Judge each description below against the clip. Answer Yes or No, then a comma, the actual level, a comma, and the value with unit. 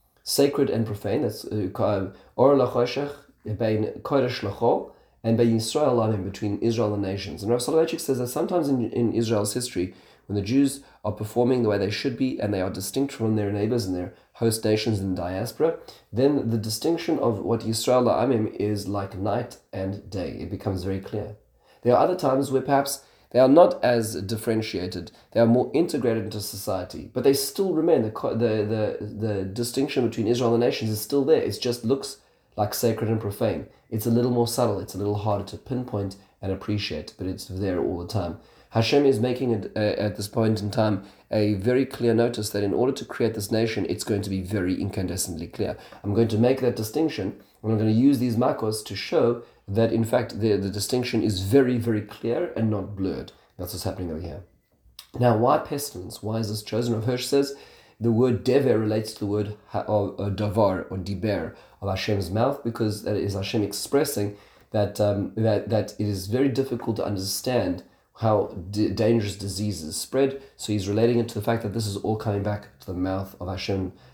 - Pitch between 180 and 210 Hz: No, low, 110 Hz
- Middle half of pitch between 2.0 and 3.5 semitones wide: Yes, average, 3.1 semitones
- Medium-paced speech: Yes, average, 195 wpm